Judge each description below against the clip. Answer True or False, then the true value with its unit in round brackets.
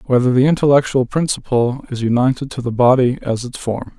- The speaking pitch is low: True (130 Hz)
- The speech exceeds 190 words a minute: False (180 wpm)